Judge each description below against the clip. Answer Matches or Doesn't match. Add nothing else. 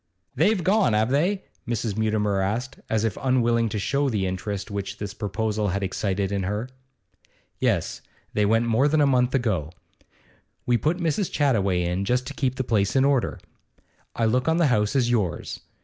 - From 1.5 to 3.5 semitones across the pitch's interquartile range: Doesn't match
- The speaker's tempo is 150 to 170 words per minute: Doesn't match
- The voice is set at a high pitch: Doesn't match